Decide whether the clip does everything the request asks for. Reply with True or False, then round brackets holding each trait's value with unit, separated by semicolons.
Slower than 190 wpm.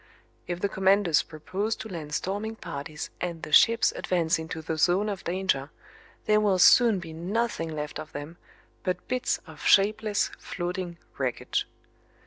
True (150 wpm)